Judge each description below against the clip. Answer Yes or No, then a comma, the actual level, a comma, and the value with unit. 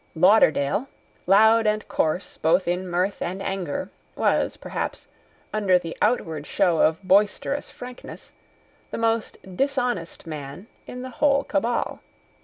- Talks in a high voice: Yes, high, 195 Hz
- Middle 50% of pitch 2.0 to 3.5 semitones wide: No, average, 4.8 semitones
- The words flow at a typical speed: No, slow, 125 wpm